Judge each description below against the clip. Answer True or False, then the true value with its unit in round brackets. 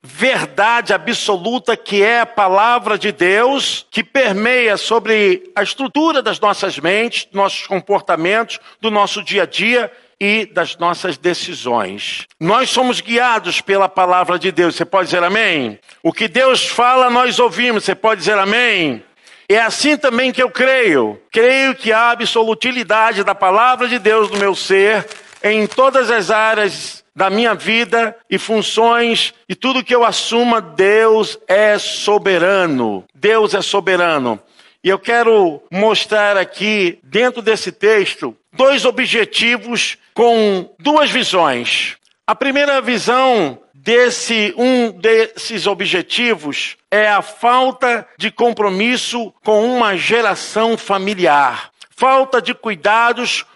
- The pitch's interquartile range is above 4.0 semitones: False (3.5 semitones)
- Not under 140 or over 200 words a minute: False (130 wpm)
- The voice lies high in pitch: True (220 Hz)